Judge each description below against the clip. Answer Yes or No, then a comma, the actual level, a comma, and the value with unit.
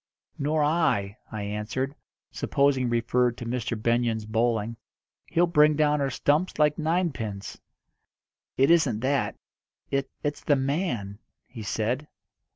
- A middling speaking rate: No, slow, 130 wpm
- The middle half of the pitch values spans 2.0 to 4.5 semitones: No, average, 4.9 semitones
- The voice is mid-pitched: No, low, 130 Hz